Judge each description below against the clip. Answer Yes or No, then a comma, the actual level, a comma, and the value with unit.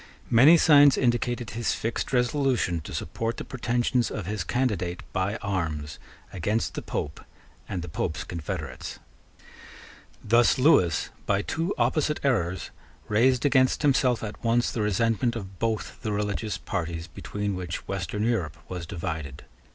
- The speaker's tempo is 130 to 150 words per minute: Yes, average, 140 wpm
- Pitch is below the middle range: Yes, low, 105 Hz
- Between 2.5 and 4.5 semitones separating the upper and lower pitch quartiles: No, average, 5.3 semitones